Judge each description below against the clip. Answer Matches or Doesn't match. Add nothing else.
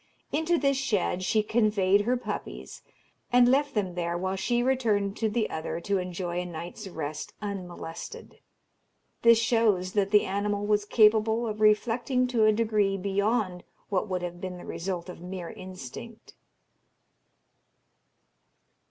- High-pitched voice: Matches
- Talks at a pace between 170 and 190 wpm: Doesn't match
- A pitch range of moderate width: Matches